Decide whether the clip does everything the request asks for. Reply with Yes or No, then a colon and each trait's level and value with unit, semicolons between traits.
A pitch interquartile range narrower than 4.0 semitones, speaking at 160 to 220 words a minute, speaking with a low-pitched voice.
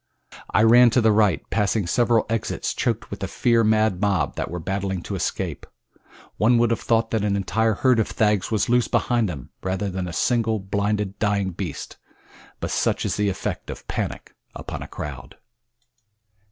Yes: average, 2.8 semitones; average, 180 wpm; low, 105 Hz